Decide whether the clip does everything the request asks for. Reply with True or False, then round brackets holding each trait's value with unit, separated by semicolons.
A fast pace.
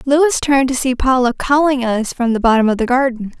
True (230 wpm)